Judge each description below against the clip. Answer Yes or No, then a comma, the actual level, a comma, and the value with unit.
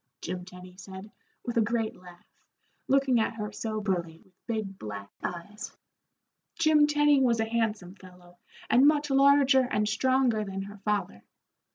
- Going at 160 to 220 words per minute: No, average, 150 wpm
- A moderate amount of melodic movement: No, wide, 5.9 semitones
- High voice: Yes, high, 215 Hz